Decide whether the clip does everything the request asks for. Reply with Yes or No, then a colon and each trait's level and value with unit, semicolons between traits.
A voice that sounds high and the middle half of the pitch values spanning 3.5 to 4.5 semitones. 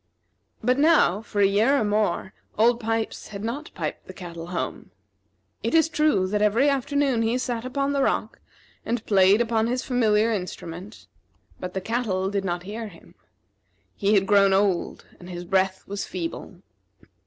Yes: high, 210 Hz; average, 4.0 semitones